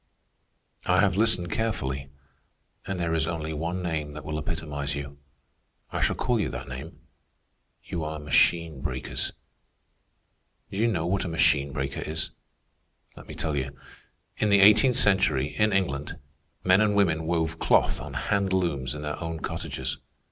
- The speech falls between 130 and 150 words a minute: No, average, 160 wpm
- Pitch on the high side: No, very low, 80 Hz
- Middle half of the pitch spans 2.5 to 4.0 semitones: No, average, 4.4 semitones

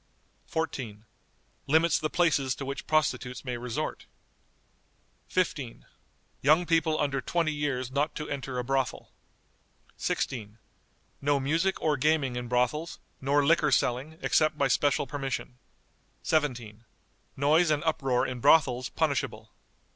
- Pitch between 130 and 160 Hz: Yes, medium, 140 Hz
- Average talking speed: No, slow, 125 wpm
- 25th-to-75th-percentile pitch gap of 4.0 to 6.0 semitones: No, average, 3.5 semitones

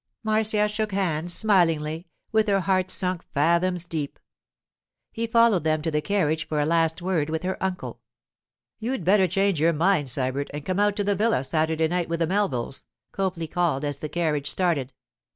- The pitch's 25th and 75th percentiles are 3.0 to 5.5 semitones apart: Yes, average, 4.0 semitones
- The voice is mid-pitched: Yes, medium, 175 Hz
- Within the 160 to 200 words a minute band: Yes, average, 180 wpm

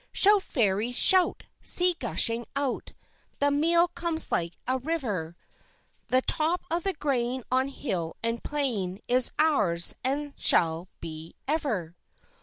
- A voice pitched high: Yes, very high, 260 Hz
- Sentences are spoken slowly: Yes, slow, 130 wpm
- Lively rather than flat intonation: Yes, wide, 8.2 semitones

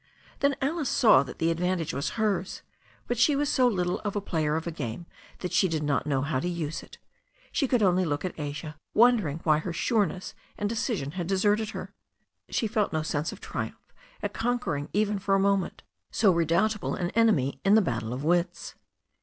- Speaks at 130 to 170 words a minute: No, average, 200 wpm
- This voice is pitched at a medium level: Yes, medium, 180 Hz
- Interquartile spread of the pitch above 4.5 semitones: Yes, wide, 5.6 semitones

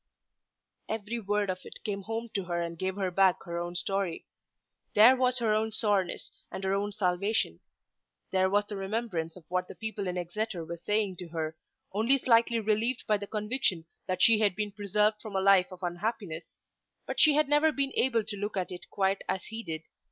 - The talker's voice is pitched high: Yes, high, 200 Hz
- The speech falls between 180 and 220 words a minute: Yes, fast, 205 wpm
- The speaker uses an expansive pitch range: No, average, 3.2 semitones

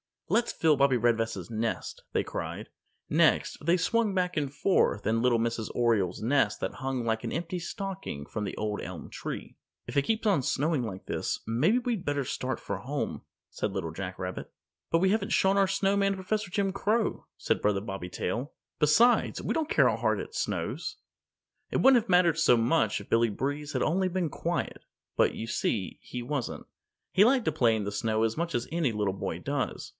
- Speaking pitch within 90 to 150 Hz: Yes, medium, 140 Hz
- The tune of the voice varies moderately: No, wide, 8.9 semitones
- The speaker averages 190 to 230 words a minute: Yes, average, 200 wpm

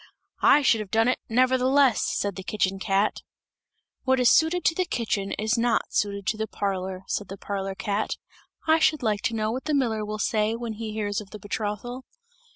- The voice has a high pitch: Yes, high, 220 Hz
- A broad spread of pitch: No, average, 3.7 semitones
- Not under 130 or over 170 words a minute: No, average, 200 wpm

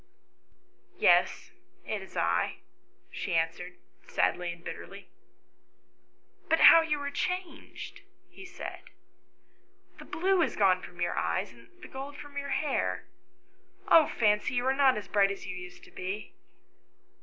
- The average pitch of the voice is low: No, high, 210 Hz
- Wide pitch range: Yes, wide, 8.2 semitones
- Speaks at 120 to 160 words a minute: Yes, average, 155 wpm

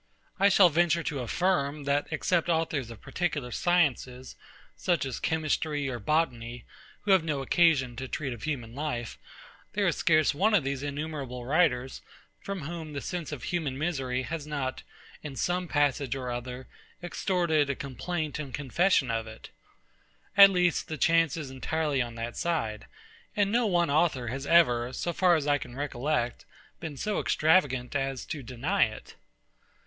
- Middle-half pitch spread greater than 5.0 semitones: No, average, 4.7 semitones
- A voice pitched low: No, medium, 145 Hz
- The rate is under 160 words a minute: No, average, 165 wpm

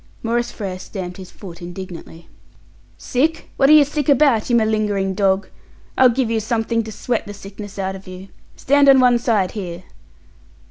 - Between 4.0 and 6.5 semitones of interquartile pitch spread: Yes, average, 4.3 semitones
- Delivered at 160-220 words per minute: Yes, average, 175 wpm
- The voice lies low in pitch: No, high, 215 Hz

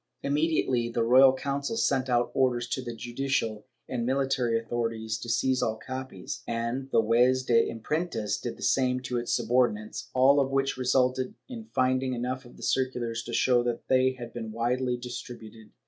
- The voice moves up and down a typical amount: No, narrow, 2.0 semitones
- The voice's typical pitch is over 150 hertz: No, low, 125 Hz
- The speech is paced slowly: No, average, 175 wpm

